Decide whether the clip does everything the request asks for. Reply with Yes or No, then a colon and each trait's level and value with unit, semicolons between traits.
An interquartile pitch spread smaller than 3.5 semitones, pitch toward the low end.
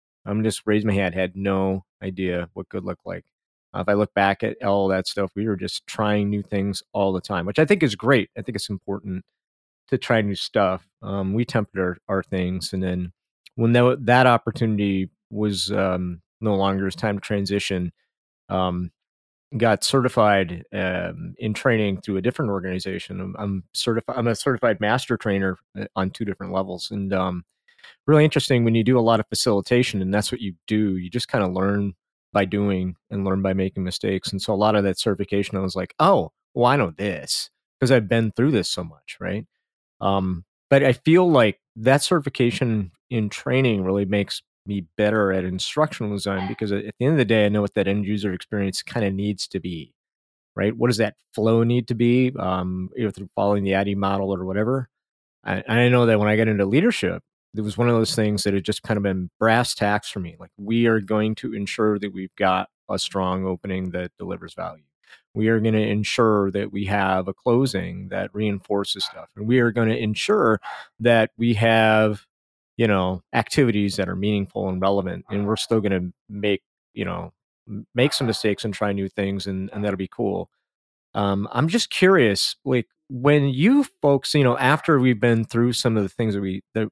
Yes: average, 3.1 semitones; low, 105 Hz